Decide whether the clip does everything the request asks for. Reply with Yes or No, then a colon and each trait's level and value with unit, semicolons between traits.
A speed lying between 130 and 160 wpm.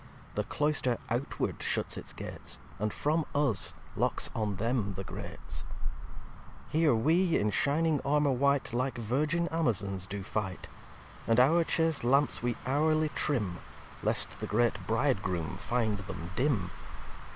Yes: average, 140 wpm